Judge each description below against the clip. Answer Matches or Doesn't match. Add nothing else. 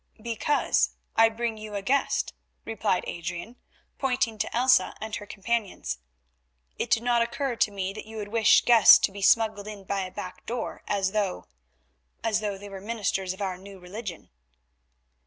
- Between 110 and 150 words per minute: Doesn't match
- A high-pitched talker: Matches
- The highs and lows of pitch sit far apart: Doesn't match